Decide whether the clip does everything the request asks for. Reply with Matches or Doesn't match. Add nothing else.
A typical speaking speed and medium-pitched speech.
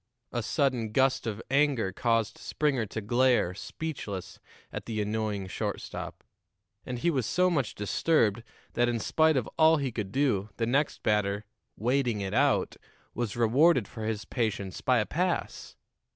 Doesn't match